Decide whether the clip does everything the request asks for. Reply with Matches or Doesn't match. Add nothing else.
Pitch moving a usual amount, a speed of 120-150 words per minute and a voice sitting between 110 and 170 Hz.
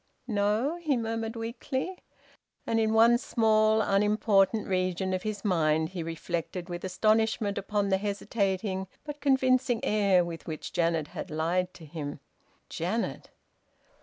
Doesn't match